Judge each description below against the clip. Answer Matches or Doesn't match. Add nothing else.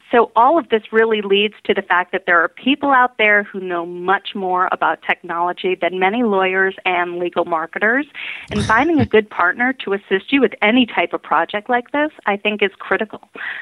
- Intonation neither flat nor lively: Matches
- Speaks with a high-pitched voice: Matches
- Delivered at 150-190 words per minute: Doesn't match